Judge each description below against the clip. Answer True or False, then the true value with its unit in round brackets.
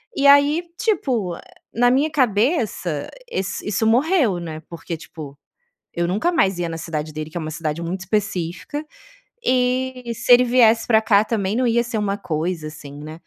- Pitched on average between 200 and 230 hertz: True (205 Hz)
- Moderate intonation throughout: False (6.9 semitones)